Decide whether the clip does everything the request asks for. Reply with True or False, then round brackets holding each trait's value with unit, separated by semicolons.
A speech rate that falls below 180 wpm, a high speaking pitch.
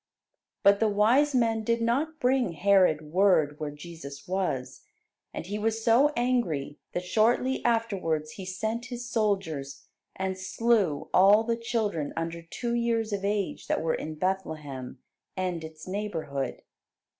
True (145 wpm; 195 Hz)